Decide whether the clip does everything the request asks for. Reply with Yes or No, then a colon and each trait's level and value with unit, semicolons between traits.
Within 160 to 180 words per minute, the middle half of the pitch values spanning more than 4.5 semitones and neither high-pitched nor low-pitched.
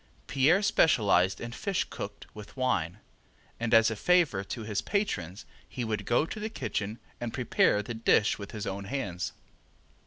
No: average, 165 wpm; average, 5.0 semitones; low, 110 Hz